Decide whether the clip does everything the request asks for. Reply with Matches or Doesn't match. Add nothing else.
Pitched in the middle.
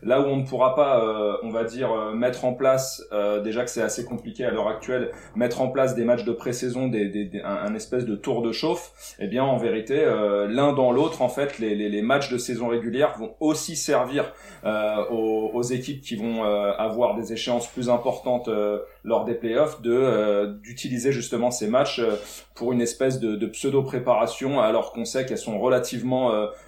Doesn't match